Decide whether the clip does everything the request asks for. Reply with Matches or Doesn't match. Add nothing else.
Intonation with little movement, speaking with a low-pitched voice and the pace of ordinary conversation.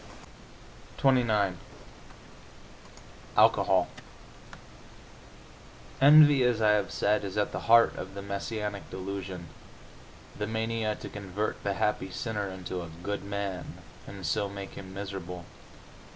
Doesn't match